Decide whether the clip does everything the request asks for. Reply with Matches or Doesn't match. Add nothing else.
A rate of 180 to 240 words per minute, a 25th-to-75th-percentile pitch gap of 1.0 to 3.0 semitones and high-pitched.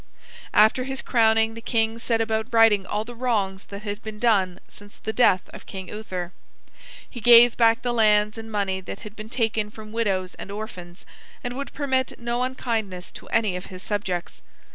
Matches